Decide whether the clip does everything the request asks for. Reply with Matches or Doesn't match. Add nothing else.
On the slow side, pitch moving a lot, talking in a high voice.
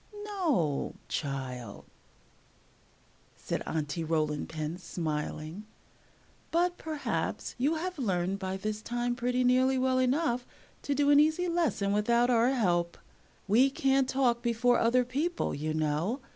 Matches